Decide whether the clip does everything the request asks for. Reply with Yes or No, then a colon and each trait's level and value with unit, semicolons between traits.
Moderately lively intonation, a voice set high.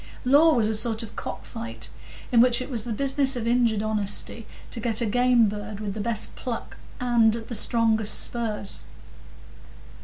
No: narrow, 2.2 semitones; high, 230 Hz